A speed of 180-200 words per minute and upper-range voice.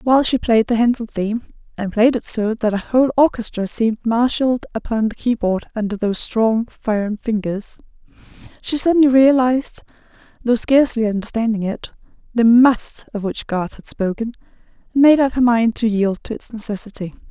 No: average, 165 wpm; high, 230 Hz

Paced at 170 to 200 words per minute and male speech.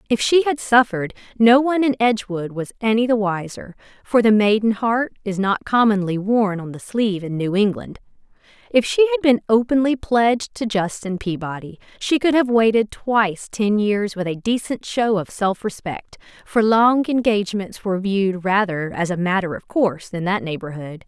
No: average, 180 wpm; female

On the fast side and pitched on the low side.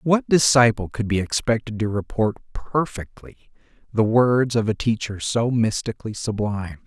No: average, 140 wpm; low, 115 Hz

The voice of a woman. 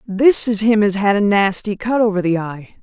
Yes: female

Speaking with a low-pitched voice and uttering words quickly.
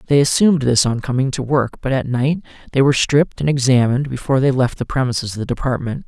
Yes: low, 130 Hz; fast, 225 wpm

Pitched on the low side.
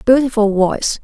No: high, 225 Hz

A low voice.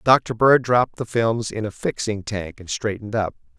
Yes: low, 110 Hz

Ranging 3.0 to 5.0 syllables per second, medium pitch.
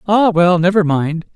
Yes: 4.4 syllables/s; medium, 180 Hz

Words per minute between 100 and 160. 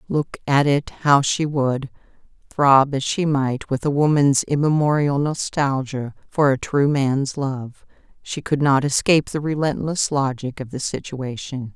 Yes: average, 155 wpm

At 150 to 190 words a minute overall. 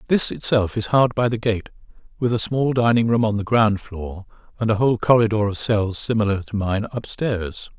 No: average, 200 wpm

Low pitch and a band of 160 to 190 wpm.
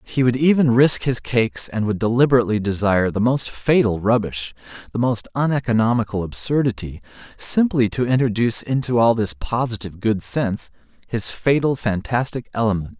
No: low, 115 Hz; average, 145 wpm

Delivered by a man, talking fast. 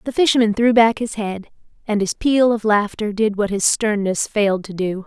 No: female; fast, 215 wpm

